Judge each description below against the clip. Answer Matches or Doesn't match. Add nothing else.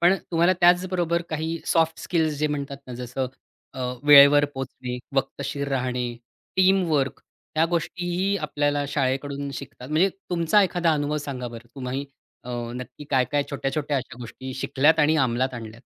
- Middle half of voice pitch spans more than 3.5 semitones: Matches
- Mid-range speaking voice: Matches